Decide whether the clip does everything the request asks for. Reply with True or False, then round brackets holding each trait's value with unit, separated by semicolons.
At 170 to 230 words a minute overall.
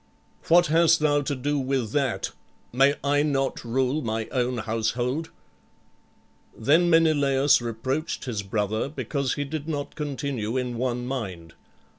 False (135 wpm)